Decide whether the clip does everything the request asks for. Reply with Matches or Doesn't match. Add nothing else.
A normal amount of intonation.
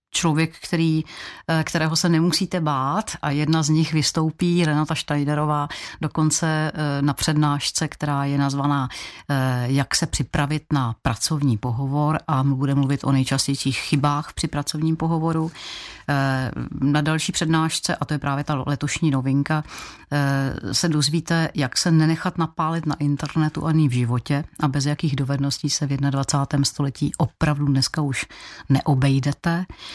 Doesn't match